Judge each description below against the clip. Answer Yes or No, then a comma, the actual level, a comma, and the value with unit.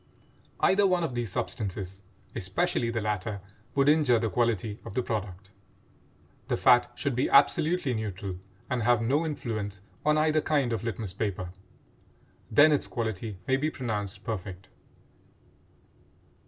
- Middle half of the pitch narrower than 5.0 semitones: No, average, 5.3 semitones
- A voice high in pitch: No, low, 115 Hz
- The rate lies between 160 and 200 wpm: No, average, 140 wpm